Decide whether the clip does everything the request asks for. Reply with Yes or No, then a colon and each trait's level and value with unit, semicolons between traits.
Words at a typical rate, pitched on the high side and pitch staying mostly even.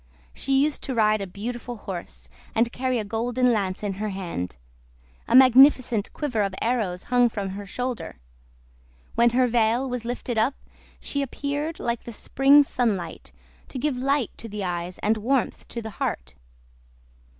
No: average, 160 wpm; high, 235 Hz; average, 4.0 semitones